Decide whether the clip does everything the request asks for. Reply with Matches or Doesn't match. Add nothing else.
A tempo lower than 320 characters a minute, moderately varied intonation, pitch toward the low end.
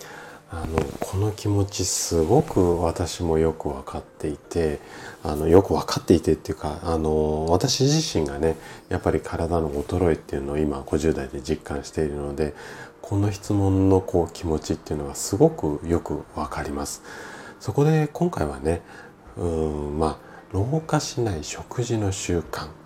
Matches